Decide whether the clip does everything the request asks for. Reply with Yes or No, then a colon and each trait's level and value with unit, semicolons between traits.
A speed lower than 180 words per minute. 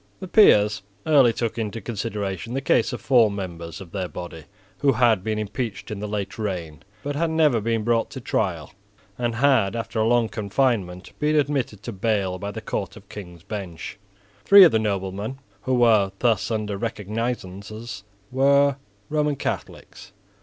Yes: average, 165 wpm